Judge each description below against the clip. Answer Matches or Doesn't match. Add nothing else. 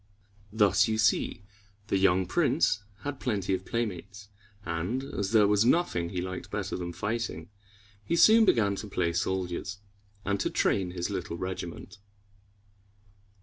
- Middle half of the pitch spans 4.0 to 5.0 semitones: Doesn't match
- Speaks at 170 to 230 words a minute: Doesn't match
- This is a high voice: Doesn't match